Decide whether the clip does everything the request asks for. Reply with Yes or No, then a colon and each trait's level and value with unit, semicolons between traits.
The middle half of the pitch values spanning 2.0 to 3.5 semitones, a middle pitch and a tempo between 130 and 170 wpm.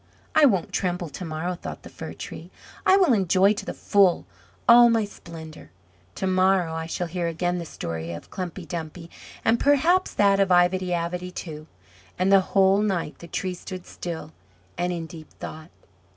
No: average, 2.7 semitones; medium, 180 Hz; average, 180 wpm